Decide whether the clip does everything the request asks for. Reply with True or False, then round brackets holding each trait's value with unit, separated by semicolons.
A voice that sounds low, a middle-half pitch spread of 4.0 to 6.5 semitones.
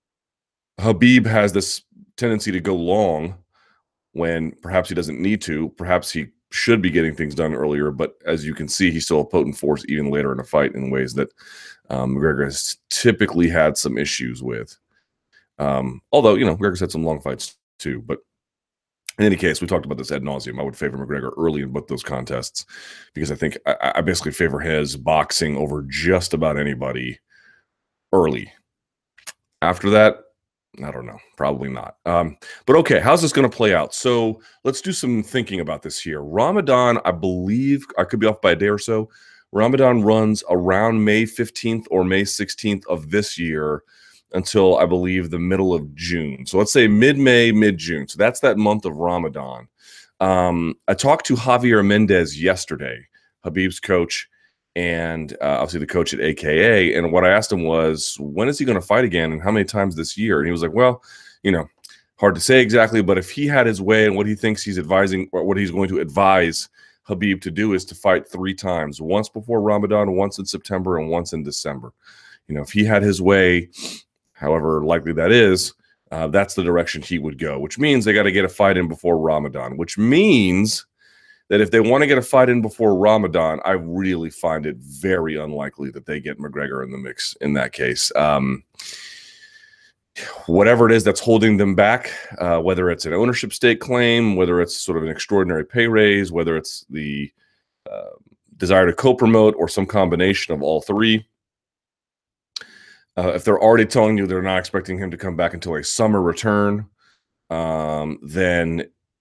True (95 Hz; 5.1 semitones)